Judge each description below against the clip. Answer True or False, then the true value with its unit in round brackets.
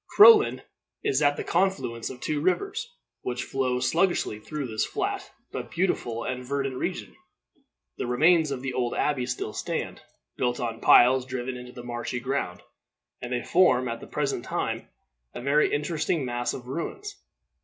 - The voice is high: False (130 Hz)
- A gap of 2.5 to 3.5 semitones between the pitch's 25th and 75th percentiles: False (3.9 semitones)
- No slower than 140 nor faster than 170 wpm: True (165 wpm)